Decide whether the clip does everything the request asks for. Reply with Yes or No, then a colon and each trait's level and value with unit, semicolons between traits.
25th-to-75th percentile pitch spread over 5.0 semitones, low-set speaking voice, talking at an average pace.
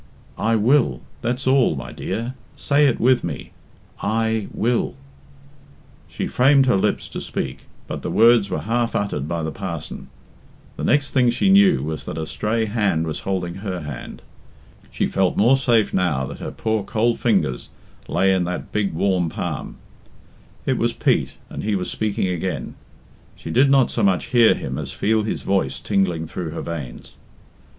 Yes: wide, 5.5 semitones; low, 100 Hz; average, 175 wpm